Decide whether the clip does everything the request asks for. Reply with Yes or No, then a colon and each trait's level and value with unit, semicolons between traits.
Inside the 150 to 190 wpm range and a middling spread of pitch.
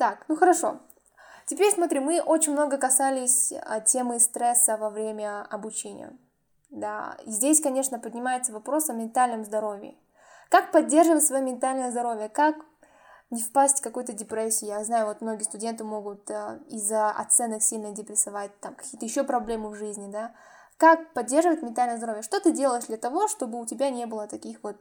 Yes: fast, 160 wpm; average, 4.6 semitones